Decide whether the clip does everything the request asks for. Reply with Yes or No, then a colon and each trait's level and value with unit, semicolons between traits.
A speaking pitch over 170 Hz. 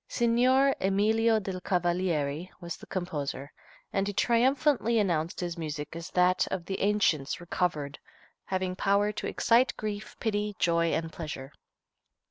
Yes: medium, 185 Hz